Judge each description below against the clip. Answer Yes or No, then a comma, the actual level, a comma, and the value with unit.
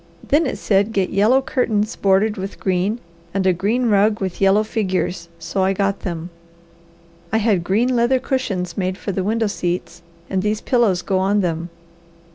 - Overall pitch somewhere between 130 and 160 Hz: No, high, 200 Hz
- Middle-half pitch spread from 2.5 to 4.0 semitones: Yes, average, 2.9 semitones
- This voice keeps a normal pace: Yes, average, 175 wpm